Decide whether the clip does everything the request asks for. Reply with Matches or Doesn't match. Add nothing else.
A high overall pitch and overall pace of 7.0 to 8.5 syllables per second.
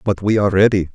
Doesn't match